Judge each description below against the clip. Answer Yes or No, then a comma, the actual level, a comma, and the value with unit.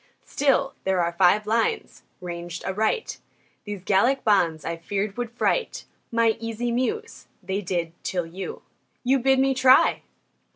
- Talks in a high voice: Yes, high, 215 Hz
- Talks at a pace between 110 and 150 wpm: Yes, average, 140 wpm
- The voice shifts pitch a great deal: Yes, wide, 6.1 semitones